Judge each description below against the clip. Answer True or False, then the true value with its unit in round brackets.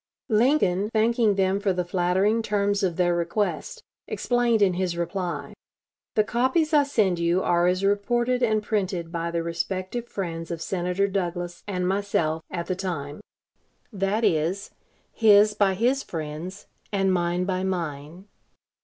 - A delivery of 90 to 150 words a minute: True (145 wpm)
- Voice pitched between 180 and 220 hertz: True (190 Hz)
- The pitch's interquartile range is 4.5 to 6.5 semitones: False (3.3 semitones)